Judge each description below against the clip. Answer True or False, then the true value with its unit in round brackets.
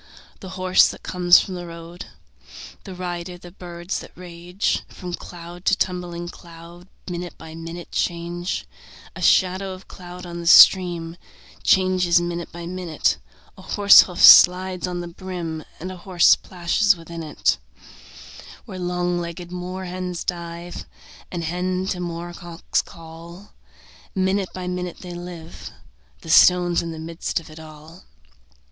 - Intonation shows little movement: True (1.2 semitones)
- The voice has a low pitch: False (175 Hz)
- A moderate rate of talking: True (145 wpm)